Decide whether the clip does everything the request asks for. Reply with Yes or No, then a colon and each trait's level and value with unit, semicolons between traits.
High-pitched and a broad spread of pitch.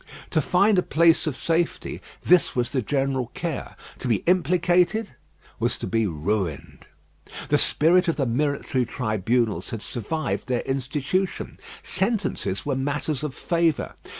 No: medium, 145 Hz; wide, 5.7 semitones